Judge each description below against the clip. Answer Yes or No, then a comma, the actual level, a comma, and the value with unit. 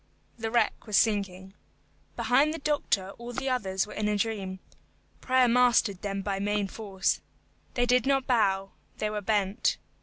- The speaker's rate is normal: Yes, average, 160 wpm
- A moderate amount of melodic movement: Yes, average, 3.9 semitones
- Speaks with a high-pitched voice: Yes, high, 210 Hz